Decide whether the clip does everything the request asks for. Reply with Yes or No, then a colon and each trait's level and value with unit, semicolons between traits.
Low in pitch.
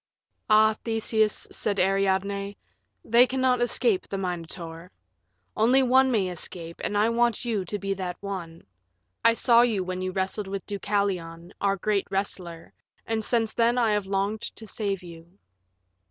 No: high, 200 Hz